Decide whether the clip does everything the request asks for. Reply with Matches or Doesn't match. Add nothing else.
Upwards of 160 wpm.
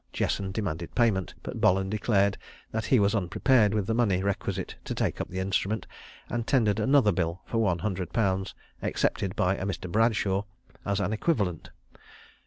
Matches